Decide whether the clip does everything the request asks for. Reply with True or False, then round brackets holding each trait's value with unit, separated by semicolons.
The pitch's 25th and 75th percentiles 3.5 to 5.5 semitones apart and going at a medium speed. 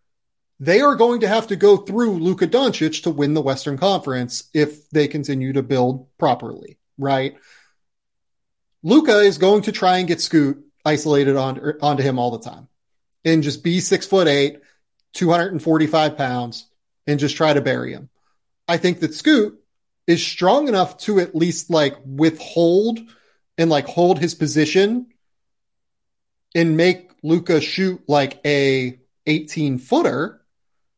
True (4.5 semitones; 145 wpm)